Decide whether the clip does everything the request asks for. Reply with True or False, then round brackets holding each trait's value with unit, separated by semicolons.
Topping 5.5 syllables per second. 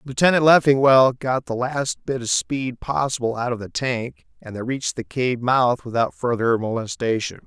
False (4.8 syllables/s)